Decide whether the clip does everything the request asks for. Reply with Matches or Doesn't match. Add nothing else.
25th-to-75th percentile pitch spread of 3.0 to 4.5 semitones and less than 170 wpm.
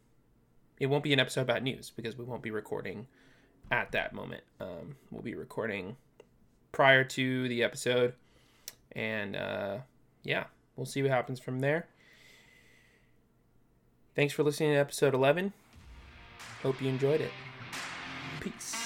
Matches